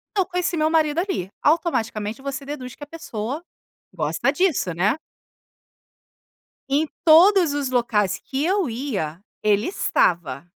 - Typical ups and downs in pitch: No, wide, 7.6 semitones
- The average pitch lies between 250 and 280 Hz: Yes, very high, 275 Hz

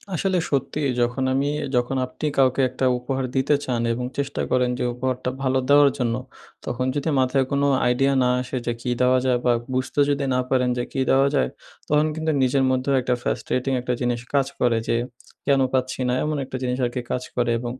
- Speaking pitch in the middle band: No, low, 130 Hz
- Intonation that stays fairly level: Yes, narrow, 1.8 semitones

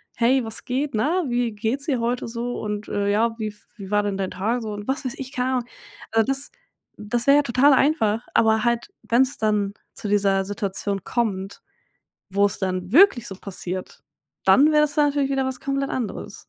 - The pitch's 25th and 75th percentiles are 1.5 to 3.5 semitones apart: No, average, 4.4 semitones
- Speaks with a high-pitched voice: Yes, high, 230 Hz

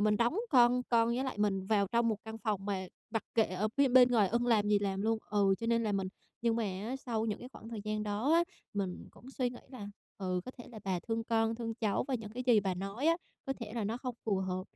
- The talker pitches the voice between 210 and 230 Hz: Yes, high, 225 Hz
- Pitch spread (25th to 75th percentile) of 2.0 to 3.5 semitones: Yes, average, 2.9 semitones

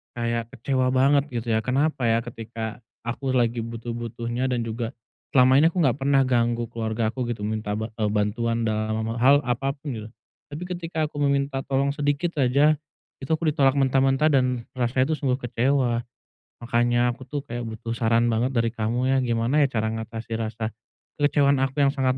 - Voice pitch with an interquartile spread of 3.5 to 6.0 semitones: No, average, 3.0 semitones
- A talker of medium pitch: No, low, 120 Hz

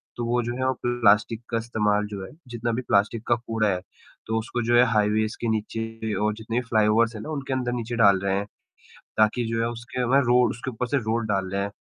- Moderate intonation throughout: No, narrow, 2.2 semitones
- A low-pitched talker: Yes, low, 115 Hz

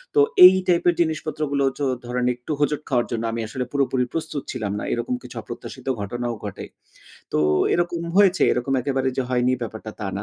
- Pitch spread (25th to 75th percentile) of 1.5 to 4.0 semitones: No, average, 4.5 semitones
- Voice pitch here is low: Yes, low, 130 Hz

